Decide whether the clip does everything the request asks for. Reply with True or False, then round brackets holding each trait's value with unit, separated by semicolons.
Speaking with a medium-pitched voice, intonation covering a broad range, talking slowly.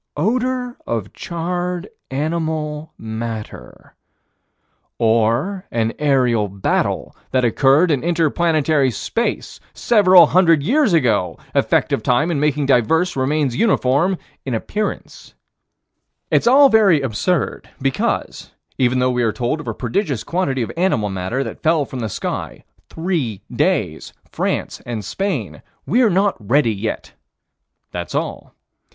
True (145 Hz; 6.9 semitones; 130 wpm)